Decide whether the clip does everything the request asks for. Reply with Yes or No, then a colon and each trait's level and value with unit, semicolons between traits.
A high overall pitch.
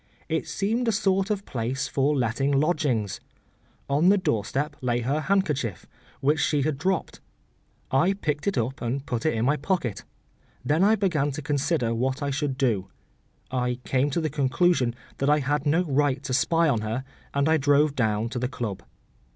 No: medium, 140 Hz